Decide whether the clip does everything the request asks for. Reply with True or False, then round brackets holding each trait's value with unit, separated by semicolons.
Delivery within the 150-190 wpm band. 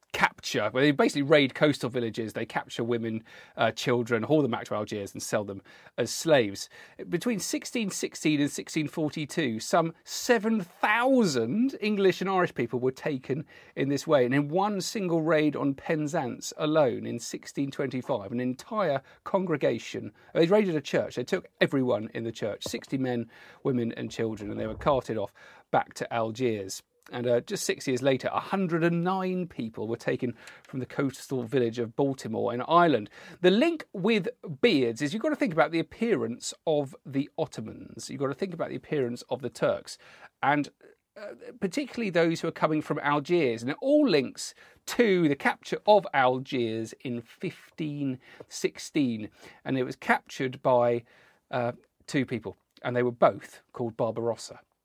True (165 wpm)